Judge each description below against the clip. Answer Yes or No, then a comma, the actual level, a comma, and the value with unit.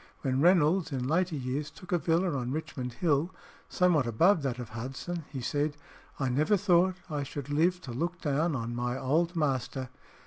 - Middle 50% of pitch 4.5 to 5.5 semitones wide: Yes, average, 4.9 semitones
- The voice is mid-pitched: Yes, medium, 145 Hz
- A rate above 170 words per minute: Yes, average, 180 wpm